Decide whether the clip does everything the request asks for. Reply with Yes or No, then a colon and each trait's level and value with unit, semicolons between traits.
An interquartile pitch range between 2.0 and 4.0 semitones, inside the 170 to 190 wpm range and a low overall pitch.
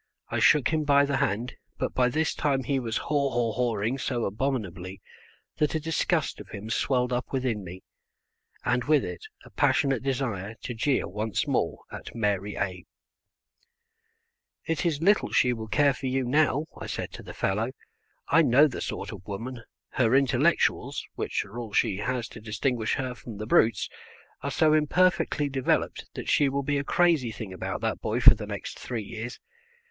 No: average, 4.4 semitones; average, 185 wpm; low, 125 Hz